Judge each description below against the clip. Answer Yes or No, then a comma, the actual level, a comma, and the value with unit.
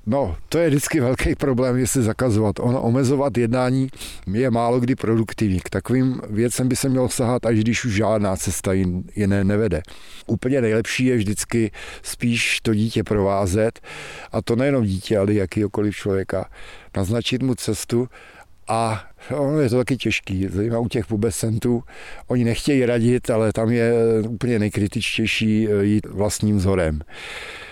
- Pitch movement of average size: Yes, average, 3.3 semitones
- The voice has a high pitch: No, low, 115 Hz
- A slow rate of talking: No, average, 145 wpm